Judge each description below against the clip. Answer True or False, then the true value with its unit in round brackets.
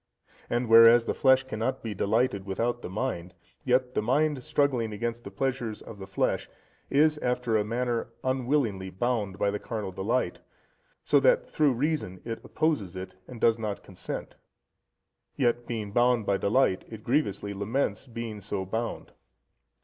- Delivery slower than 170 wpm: True (155 wpm)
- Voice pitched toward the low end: True (115 Hz)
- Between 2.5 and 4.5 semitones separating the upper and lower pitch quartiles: True (4.1 semitones)